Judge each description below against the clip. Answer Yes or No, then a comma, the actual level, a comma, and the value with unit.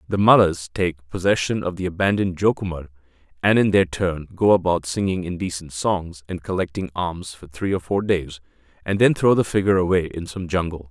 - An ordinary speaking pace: Yes, average, 185 wpm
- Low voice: Yes, very low, 90 Hz